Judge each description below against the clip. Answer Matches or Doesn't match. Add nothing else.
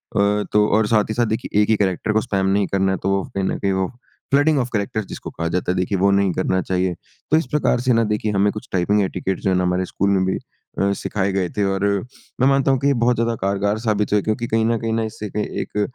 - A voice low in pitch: Matches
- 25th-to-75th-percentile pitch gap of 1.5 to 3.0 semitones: Matches